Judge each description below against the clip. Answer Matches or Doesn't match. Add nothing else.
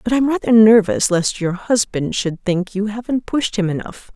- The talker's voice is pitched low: Doesn't match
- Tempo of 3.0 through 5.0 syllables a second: Matches